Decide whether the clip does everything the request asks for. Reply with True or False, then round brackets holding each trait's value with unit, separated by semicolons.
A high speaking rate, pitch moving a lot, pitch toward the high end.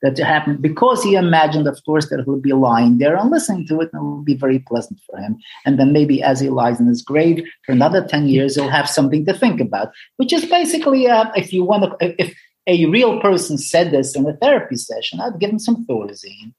False (245 wpm; 7.2 semitones; 155 Hz)